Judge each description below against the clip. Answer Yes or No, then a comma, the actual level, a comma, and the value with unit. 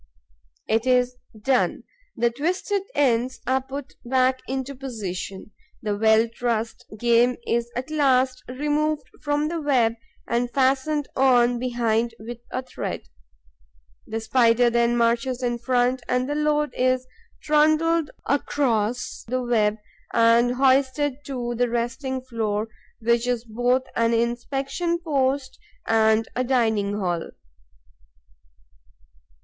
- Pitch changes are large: No, narrow, 2.5 semitones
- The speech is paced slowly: Yes, slow, 120 wpm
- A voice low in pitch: No, very high, 250 Hz